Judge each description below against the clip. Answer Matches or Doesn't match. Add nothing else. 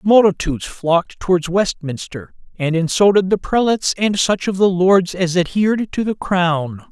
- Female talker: Doesn't match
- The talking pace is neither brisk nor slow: Matches